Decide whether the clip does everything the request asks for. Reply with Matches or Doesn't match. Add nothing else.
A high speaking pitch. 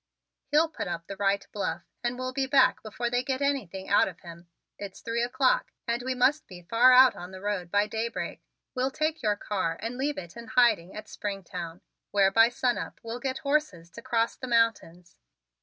Matches